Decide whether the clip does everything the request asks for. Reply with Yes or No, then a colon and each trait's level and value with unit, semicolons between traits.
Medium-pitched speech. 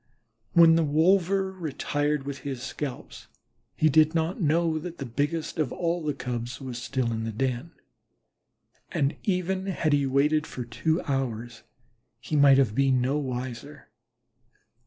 Yes: medium, 145 Hz